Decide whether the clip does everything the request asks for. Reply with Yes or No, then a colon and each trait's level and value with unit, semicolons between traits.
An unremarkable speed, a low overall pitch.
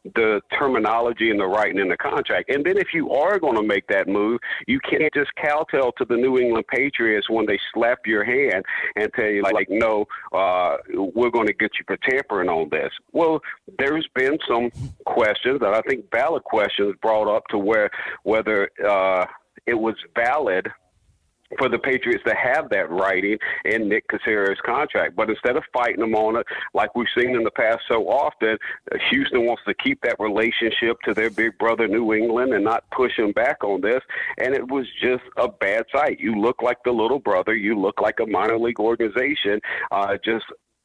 Yes: average, 195 wpm; low, 115 Hz